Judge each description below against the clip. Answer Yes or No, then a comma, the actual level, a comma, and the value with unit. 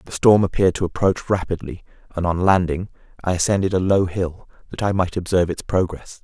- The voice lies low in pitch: Yes, very low, 90 Hz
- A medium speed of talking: Yes, average, 195 wpm